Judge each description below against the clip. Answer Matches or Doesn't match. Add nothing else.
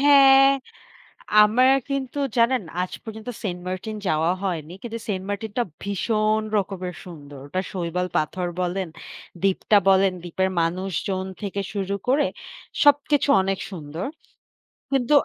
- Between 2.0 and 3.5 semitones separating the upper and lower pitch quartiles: Doesn't match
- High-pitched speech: Matches